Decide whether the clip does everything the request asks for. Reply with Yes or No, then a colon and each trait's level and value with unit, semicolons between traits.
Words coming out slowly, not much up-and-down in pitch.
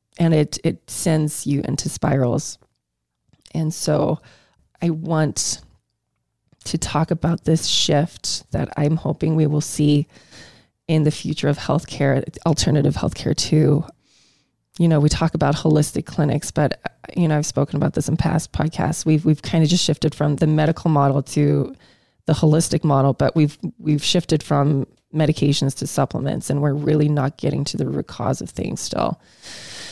No: average, 160 wpm; narrow, 1.9 semitones